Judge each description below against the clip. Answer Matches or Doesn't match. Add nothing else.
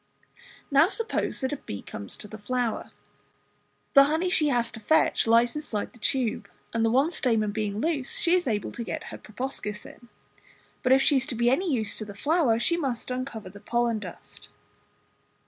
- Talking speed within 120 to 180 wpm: Doesn't match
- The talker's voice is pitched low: Doesn't match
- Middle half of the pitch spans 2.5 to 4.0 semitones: Doesn't match